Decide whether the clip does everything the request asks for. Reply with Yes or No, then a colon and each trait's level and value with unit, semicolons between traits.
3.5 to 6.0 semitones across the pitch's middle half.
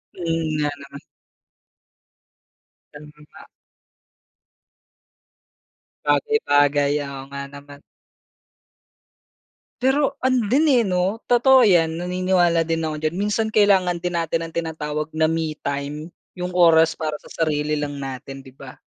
Yes: average, 3.8 semitones